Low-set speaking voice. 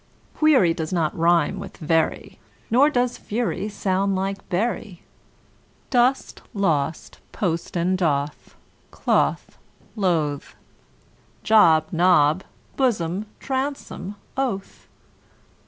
No: high, 190 Hz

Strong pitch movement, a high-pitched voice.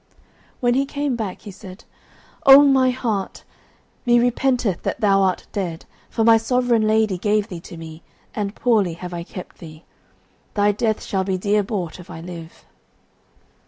No: average, 4.6 semitones; high, 205 Hz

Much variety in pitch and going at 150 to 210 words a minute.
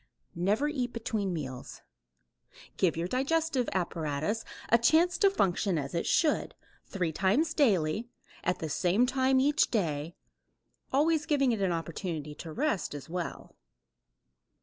No: wide, 8.2 semitones; slow, 135 wpm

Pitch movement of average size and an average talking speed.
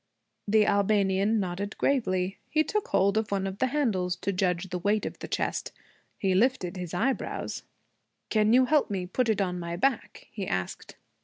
Yes: average, 3.4 semitones; average, 180 wpm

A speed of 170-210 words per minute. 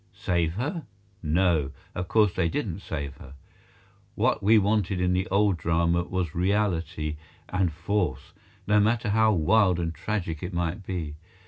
No: average, 150 wpm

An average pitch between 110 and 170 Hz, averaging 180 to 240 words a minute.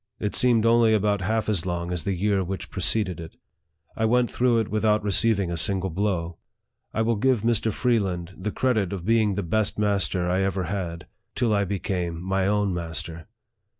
No: low, 100 Hz; average, 185 wpm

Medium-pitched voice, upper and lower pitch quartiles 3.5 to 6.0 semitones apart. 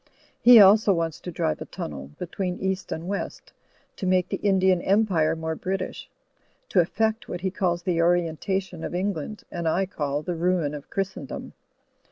No: medium, 180 Hz; average, 2.8 semitones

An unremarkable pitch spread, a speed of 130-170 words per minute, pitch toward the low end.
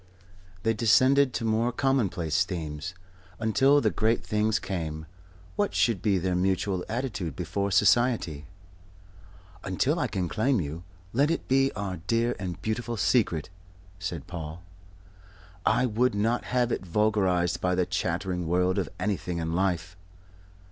Yes: average, 4.7 semitones; average, 140 wpm; very low, 95 Hz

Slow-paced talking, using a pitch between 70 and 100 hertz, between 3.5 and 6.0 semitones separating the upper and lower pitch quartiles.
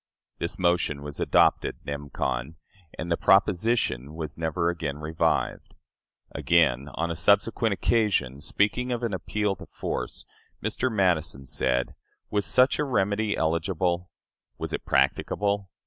Yes: slow, 130 wpm; very low, 85 Hz; average, 5.1 semitones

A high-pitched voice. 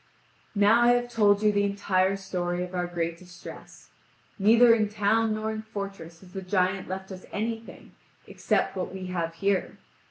Yes: high, 195 Hz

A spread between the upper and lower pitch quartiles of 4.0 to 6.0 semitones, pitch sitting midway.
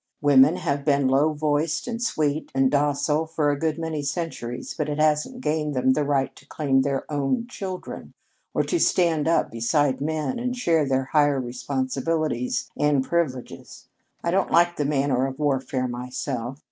No: average, 3.0 semitones; medium, 145 Hz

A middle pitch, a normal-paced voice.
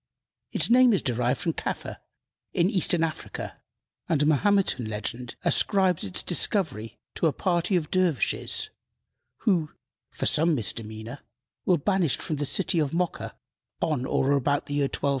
Yes: medium, 155 Hz; average, 150 wpm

